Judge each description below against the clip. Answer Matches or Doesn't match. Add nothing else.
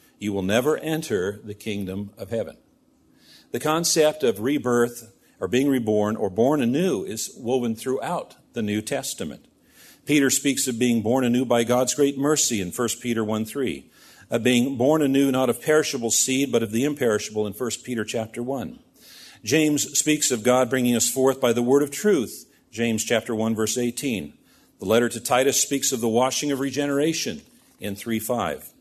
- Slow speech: Doesn't match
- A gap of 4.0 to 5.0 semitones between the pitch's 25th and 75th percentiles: Doesn't match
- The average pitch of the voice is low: Matches